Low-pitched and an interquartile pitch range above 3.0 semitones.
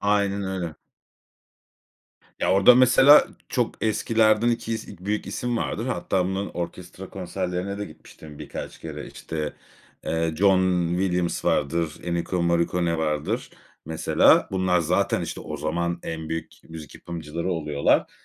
Yes: very low, 90 Hz; average, 3.4 semitones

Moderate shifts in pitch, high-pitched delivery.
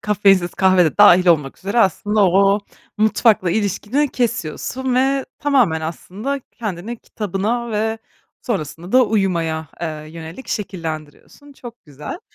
No: wide, 5.8 semitones; high, 200 Hz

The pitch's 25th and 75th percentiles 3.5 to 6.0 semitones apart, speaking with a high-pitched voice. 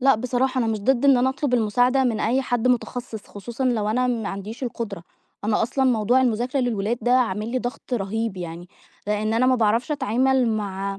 No: average, 3.1 semitones; high, 235 Hz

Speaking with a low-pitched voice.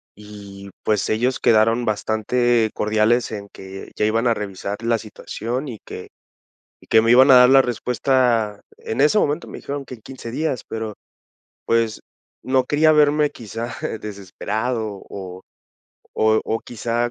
Yes: low, 115 Hz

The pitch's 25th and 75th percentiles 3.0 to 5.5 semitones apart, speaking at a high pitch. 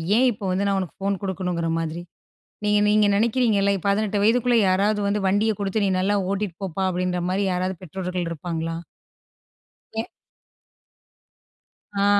No: narrow, 2.4 semitones; high, 195 Hz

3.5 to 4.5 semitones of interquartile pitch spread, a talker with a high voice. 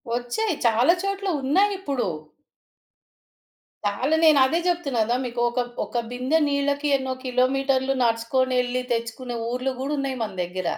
No: average, 2.8 semitones; very high, 260 Hz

